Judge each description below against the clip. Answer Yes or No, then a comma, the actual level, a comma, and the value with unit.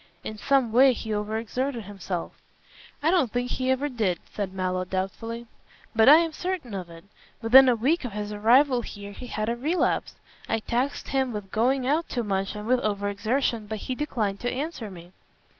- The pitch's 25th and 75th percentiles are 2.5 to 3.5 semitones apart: No, average, 4.2 semitones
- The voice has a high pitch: Yes, high, 230 Hz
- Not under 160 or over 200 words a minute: Yes, average, 195 wpm